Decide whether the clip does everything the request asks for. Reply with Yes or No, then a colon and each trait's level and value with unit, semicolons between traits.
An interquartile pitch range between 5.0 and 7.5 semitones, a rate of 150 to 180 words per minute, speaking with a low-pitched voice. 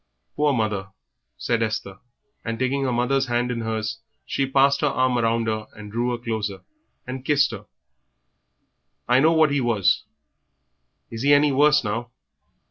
No: average, 3.4 semitones; average, 155 wpm; low, 120 Hz